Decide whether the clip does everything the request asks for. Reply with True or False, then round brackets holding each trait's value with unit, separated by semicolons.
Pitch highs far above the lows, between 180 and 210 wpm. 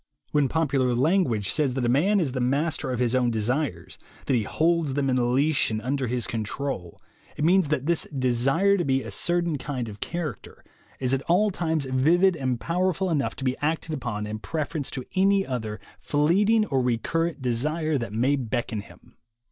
False (4.9 semitones; 190 wpm)